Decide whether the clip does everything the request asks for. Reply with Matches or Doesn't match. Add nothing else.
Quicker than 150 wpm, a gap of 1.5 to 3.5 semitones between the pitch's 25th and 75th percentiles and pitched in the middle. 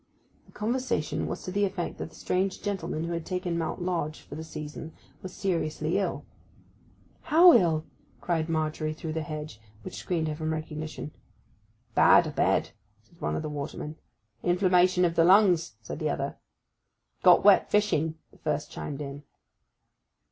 Matches